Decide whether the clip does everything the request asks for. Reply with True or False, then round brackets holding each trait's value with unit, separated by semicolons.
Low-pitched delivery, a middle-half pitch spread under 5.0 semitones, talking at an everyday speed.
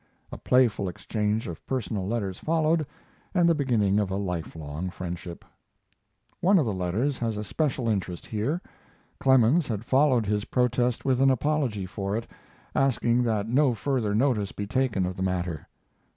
False (110 Hz; 5.4 semitones; 160 wpm)